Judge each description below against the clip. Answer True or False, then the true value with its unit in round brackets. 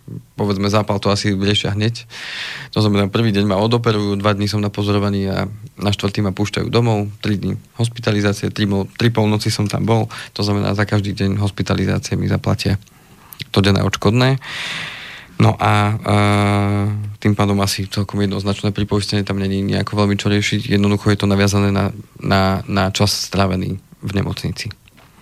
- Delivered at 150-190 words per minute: True (160 wpm)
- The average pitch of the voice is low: True (105 Hz)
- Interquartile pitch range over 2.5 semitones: False (1.0 semitones)